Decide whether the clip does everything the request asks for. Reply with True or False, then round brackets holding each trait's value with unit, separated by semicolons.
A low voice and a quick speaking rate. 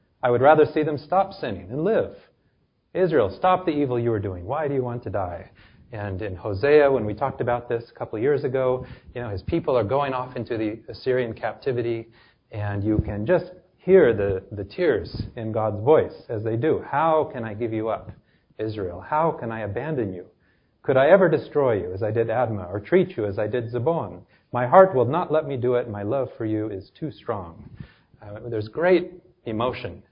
True (120 Hz; 215 wpm)